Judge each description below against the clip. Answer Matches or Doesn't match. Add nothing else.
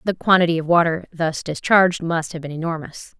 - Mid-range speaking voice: Matches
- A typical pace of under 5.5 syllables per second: Doesn't match